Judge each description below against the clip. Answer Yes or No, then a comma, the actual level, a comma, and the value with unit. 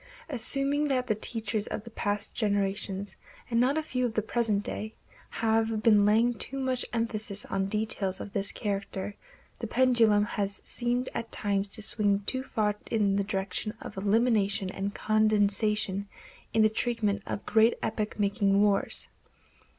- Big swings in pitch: No, narrow, 2.4 semitones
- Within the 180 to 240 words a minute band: No, average, 160 wpm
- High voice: Yes, high, 215 Hz